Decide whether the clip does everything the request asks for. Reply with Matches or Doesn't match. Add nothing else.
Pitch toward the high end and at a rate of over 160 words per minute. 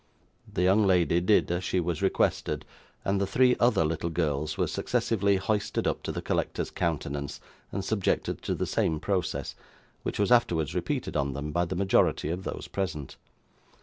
Doesn't match